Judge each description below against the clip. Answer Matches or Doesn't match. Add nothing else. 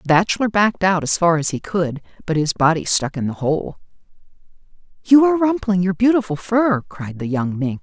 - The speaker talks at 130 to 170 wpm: Doesn't match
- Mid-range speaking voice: Matches